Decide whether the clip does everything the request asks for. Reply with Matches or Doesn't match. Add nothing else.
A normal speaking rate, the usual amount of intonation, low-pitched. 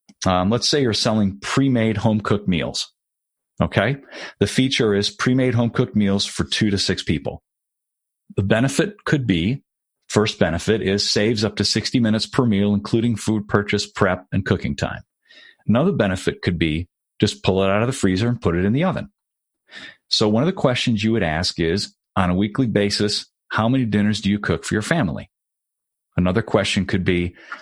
Matches